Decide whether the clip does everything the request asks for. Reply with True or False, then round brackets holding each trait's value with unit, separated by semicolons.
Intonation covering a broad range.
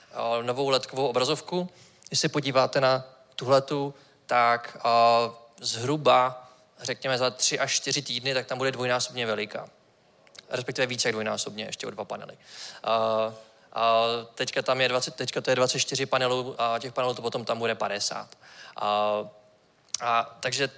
False (2.4 semitones)